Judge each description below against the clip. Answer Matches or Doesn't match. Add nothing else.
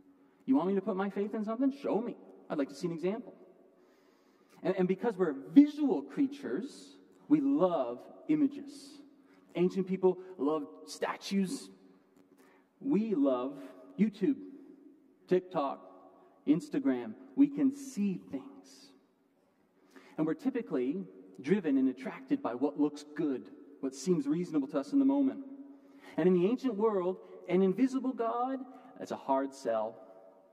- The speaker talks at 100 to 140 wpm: Matches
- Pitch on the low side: Doesn't match